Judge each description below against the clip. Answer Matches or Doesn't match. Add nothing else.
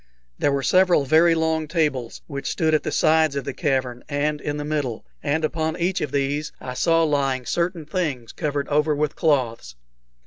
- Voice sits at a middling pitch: Matches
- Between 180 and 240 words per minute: Matches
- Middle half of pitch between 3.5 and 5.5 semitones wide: Doesn't match